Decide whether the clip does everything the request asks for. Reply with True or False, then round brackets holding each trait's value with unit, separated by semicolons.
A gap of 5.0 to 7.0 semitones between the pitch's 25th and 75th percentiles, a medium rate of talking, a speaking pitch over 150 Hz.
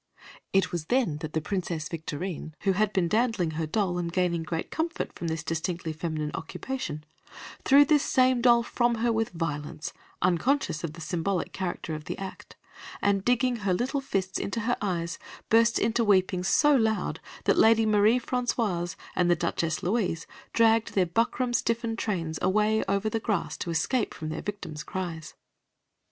True (5.5 semitones; 170 wpm; 190 Hz)